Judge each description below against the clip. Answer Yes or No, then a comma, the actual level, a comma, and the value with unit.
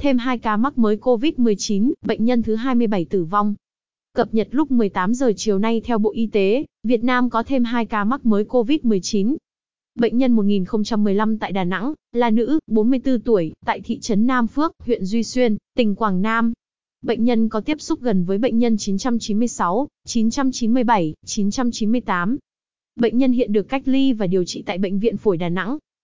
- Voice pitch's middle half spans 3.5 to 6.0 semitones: No, average, 3.0 semitones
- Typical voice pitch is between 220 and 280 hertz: Yes, high, 230 Hz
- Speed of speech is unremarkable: Yes, average, 185 wpm